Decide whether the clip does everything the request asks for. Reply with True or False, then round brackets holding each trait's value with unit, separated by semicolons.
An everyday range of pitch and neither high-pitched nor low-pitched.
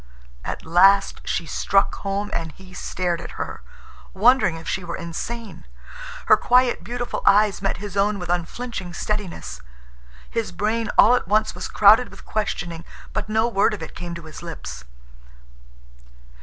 False (3.8 semitones; 195 Hz)